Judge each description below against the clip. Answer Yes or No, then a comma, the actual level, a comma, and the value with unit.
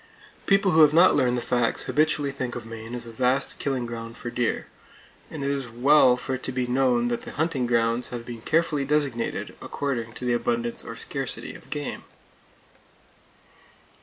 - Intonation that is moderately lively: Yes, average, 3.1 semitones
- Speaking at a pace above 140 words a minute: Yes, average, 185 wpm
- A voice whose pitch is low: Yes, low, 125 Hz